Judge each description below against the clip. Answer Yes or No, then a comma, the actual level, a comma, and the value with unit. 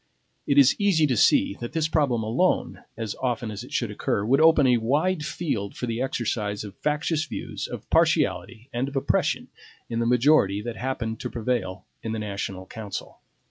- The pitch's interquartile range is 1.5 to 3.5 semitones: No, average, 4.7 semitones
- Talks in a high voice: No, low, 120 Hz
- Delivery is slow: No, average, 185 wpm